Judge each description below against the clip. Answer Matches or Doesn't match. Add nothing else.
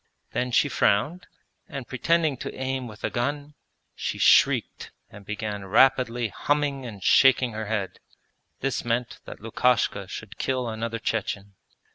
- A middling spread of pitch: Matches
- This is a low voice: Matches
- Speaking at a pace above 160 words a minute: Doesn't match